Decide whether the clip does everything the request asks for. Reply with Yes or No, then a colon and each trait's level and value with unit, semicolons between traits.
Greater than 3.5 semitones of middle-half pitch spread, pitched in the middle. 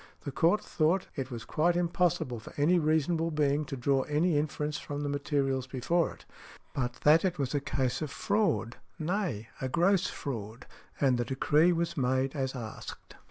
Yes: average, 4.1 semitones; medium, 145 Hz